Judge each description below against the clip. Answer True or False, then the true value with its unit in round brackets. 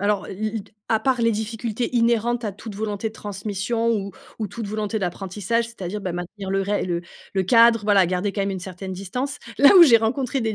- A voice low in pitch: False (210 Hz)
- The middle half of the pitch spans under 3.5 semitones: True (2.9 semitones)